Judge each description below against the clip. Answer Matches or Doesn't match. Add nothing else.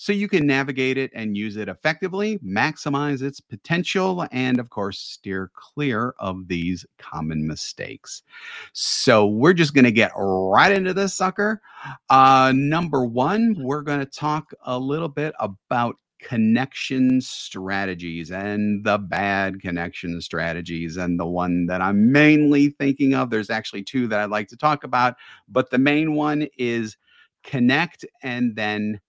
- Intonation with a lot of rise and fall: Matches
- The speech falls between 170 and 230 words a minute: Doesn't match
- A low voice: Matches